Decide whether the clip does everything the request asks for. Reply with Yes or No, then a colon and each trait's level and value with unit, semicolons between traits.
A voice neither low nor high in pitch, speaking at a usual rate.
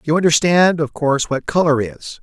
Yes: medium, 155 Hz; average, 190 wpm